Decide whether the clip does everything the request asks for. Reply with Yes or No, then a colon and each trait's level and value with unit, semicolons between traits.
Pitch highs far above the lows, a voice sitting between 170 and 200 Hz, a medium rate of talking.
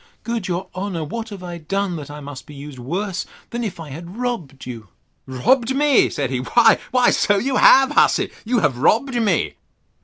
Yes: wide, 8.1 semitones; medium, 185 Hz; average, 190 wpm